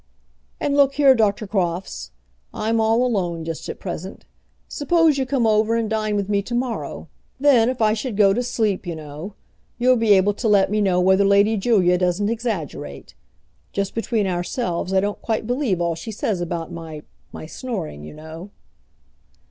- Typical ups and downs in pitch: Yes, average, 4.4 semitones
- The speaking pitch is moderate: No, high, 205 Hz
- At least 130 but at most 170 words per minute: No, average, 180 wpm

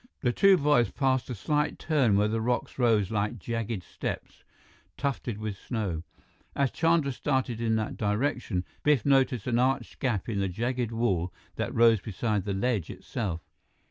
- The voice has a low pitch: Yes, low, 115 Hz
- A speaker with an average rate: Yes, average, 165 wpm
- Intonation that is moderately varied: Yes, average, 4.1 semitones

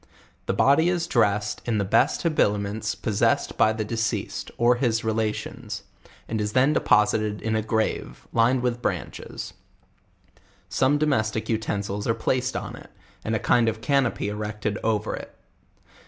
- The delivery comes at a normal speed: Yes, average, 155 wpm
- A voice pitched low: Yes, low, 110 Hz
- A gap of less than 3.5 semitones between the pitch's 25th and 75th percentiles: Yes, narrow, 2.6 semitones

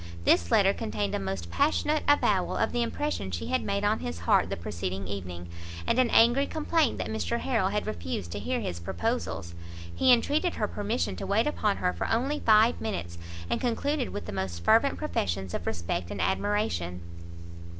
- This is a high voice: Yes, high, 195 Hz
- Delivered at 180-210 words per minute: Yes, average, 185 wpm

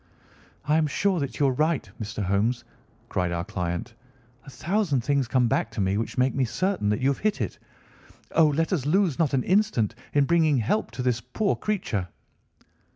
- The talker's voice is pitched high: No, low, 135 Hz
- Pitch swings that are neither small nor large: No, wide, 6.3 semitones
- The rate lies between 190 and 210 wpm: Yes, average, 195 wpm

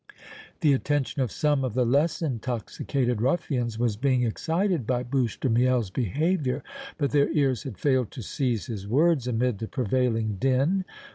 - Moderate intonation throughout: Yes, average, 3.3 semitones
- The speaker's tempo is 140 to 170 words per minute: Yes, average, 160 wpm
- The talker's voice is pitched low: Yes, low, 130 Hz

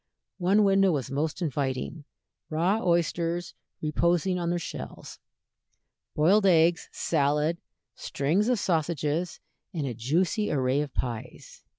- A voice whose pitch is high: No, medium, 165 Hz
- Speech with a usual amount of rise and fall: Yes, average, 3.5 semitones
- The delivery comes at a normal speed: No, slow, 115 wpm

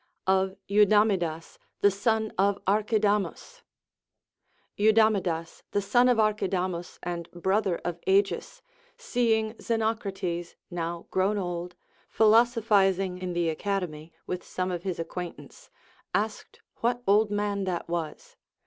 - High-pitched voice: Yes, high, 195 Hz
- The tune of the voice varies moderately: Yes, average, 3.4 semitones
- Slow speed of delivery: Yes, slow, 115 wpm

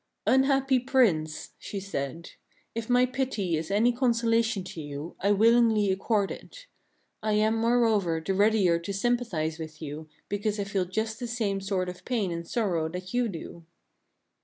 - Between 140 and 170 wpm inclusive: Yes, average, 165 wpm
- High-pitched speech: Yes, high, 205 Hz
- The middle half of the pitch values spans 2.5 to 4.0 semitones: No, average, 5.2 semitones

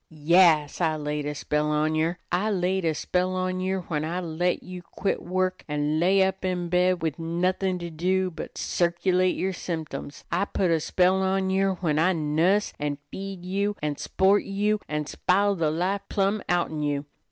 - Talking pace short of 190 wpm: No, average, 195 wpm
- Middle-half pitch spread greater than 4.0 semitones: No, average, 3.1 semitones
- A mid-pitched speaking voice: Yes, medium, 180 Hz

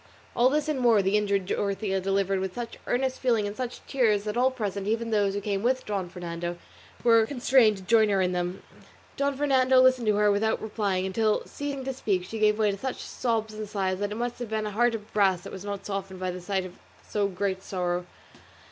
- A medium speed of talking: No, fast, 230 wpm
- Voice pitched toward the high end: Yes, high, 210 Hz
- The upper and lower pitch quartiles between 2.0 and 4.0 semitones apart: Yes, average, 3.6 semitones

